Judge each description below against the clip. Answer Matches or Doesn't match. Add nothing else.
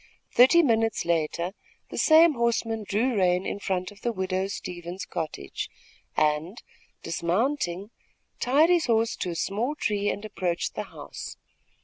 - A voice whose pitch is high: Matches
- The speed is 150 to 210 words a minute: Doesn't match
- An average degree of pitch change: Matches